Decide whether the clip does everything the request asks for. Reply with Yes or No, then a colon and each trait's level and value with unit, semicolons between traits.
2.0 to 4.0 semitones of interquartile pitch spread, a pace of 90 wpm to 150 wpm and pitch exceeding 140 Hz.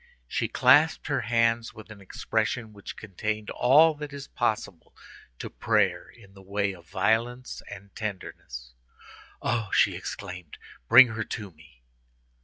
No: average, 3.5 semitones; average, 140 wpm; low, 110 Hz